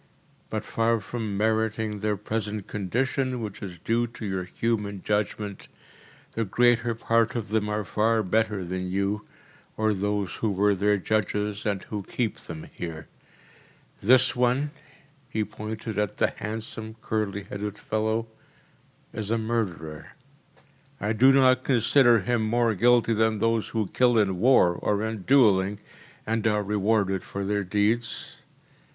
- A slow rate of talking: No, average, 145 wpm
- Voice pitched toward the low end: Yes, low, 110 Hz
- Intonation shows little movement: Yes, narrow, 2.1 semitones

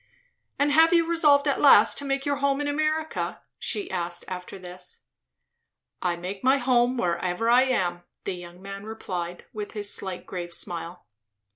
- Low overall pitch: No, high, 210 Hz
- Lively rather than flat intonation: Yes, wide, 7.9 semitones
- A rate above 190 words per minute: No, average, 165 wpm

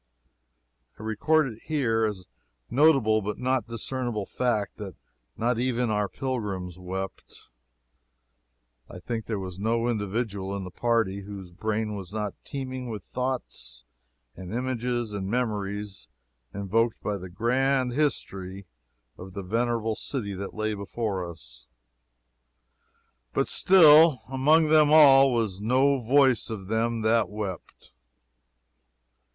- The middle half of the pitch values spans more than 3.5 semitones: Yes, average, 4.2 semitones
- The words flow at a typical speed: No, slow, 125 wpm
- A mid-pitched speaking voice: No, low, 110 Hz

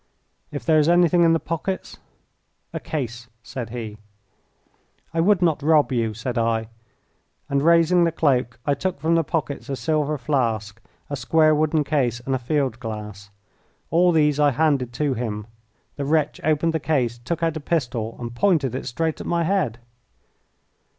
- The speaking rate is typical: Yes, average, 175 wpm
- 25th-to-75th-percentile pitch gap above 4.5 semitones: Yes, average, 5.2 semitones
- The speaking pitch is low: No, medium, 145 Hz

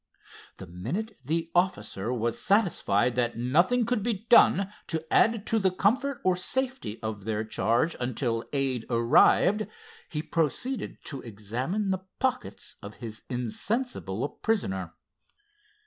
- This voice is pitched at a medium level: Yes, medium, 150 Hz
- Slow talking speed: Yes, slow, 130 wpm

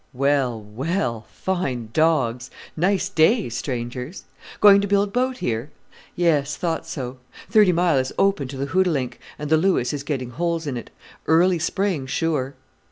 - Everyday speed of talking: Yes, average, 155 wpm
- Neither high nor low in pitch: Yes, medium, 150 Hz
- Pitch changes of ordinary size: No, wide, 6.0 semitones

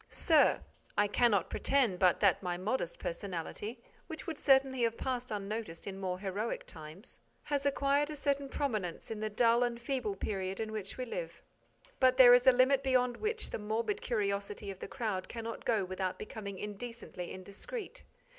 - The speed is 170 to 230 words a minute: Yes, average, 175 wpm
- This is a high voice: Yes, high, 225 Hz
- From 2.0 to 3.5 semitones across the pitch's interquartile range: No, average, 4.8 semitones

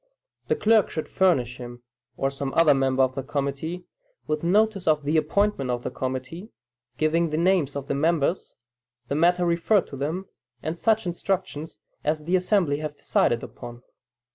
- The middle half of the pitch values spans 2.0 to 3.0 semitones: No, average, 4.5 semitones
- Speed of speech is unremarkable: Yes, average, 165 wpm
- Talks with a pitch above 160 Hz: No, medium, 155 Hz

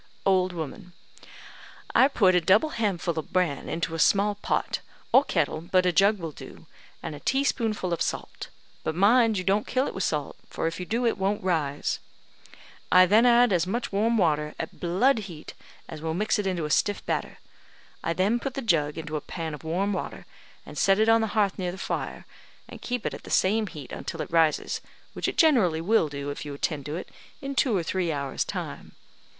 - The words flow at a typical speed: No, fast, 210 wpm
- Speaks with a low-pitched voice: No, medium, 185 Hz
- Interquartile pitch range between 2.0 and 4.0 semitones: No, average, 4.9 semitones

